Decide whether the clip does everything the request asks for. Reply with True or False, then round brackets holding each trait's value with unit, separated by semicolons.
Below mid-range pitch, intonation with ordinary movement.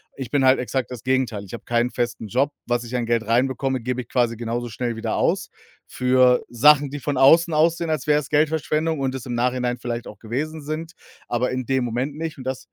True (130 Hz; 3.3 semitones)